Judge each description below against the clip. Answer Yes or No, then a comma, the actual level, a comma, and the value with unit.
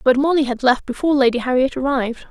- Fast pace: Yes, fast, 210 wpm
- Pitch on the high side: Yes, very high, 265 Hz